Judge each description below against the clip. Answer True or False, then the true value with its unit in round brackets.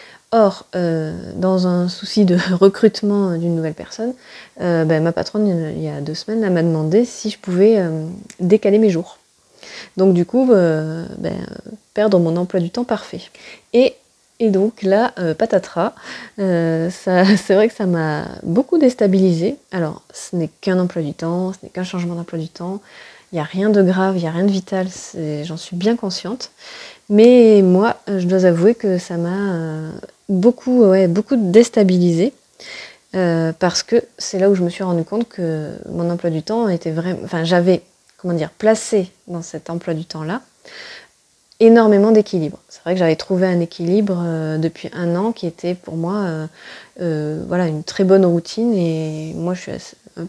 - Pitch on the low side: False (185 Hz)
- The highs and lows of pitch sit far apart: False (3.7 semitones)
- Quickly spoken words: False (185 wpm)